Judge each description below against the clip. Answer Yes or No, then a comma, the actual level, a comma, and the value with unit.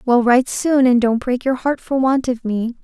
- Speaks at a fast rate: Yes, fast, 255 wpm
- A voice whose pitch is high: Yes, very high, 250 Hz